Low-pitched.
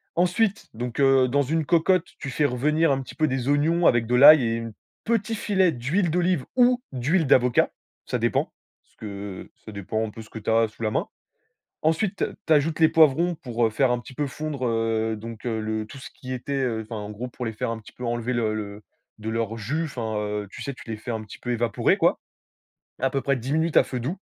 Yes: low, 125 Hz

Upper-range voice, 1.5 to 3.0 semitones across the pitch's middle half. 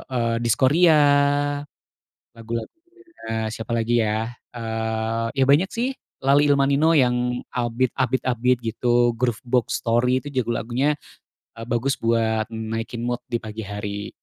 No: low, 120 Hz; narrow, 2.6 semitones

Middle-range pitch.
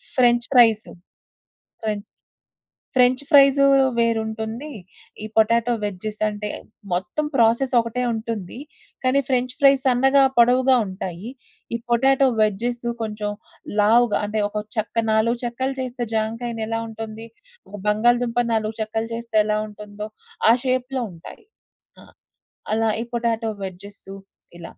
No: high, 230 Hz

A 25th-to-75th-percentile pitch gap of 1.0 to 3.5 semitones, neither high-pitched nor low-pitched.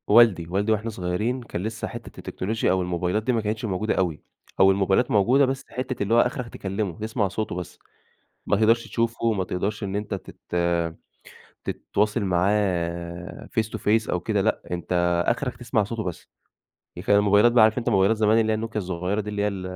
No: average, 3.2 semitones; low, 105 Hz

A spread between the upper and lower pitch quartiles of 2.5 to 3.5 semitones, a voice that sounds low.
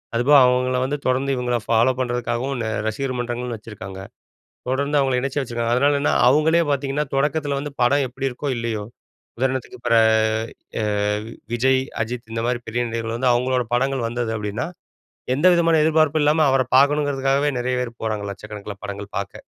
Yes: average, 3.1 semitones; low, 125 Hz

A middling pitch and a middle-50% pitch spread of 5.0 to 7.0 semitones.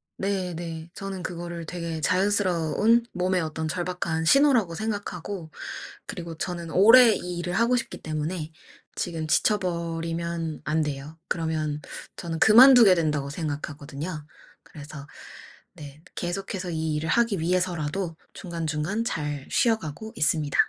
No: medium, 170 Hz; average, 3.2 semitones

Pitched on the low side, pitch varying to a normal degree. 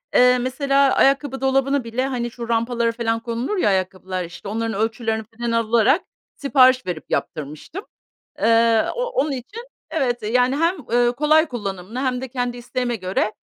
No: high, 245 Hz; average, 3.0 semitones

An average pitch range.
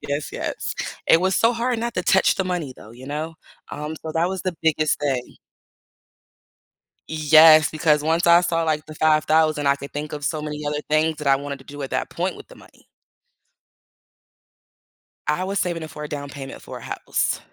No: narrow, 2.3 semitones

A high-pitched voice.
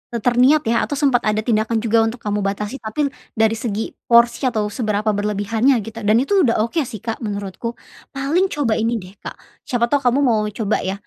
Yes: high, 225 Hz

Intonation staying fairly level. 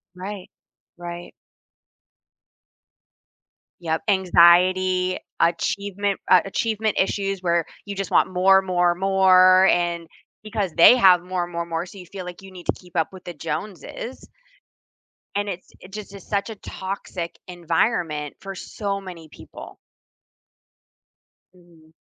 Yes: narrow, 2.2 semitones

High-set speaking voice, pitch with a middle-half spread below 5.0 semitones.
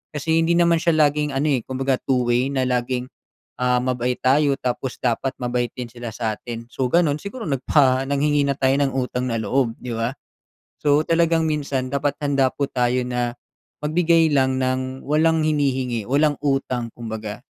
No: low, 130 Hz; average, 2.9 semitones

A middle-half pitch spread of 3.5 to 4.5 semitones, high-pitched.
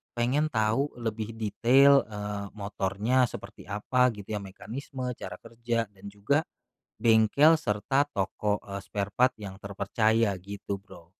No: average, 3.8 semitones; low, 110 Hz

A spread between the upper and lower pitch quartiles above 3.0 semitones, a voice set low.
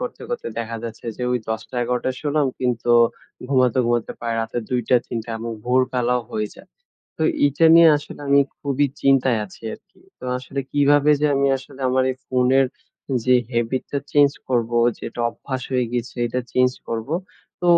No: average, 2.7 semitones; low, 125 Hz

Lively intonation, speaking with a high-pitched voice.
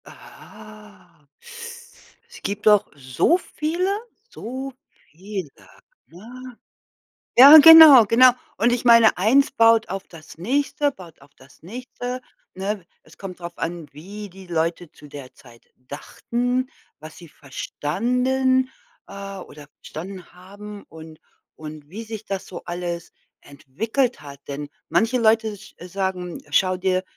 Yes: wide, 6.5 semitones; high, 195 Hz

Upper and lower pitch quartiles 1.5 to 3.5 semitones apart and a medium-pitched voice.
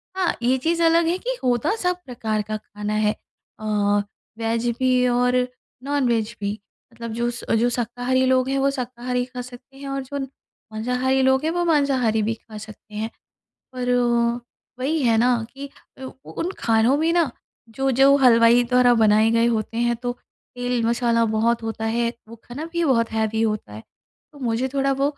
No: average, 2.8 semitones; high, 245 Hz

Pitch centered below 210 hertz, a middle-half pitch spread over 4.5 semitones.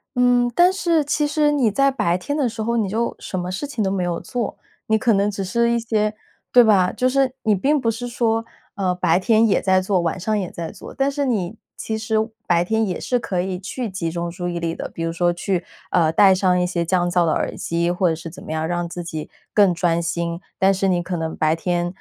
Yes: high, 190 Hz; average, 5.1 semitones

